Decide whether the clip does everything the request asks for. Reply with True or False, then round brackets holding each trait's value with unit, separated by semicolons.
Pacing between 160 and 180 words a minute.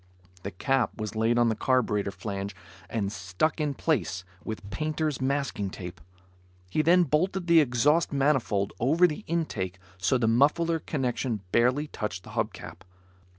False (150 wpm)